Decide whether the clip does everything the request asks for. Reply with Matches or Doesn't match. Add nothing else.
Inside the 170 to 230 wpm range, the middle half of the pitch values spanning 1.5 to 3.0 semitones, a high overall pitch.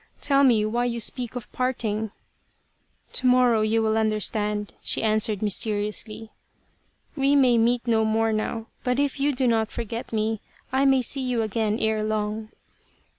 Matches